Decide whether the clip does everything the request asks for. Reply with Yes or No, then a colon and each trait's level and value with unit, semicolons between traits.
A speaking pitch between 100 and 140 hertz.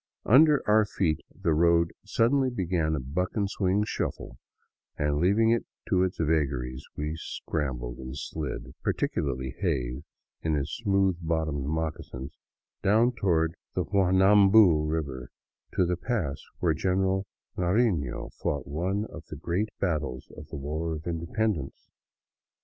No: very low, 85 Hz